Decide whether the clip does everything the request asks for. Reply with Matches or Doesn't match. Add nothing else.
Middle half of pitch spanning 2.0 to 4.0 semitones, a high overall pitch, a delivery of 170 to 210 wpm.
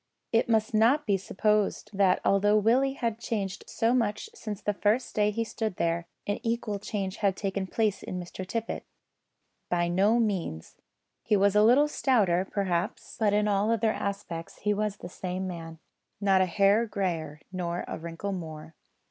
Matches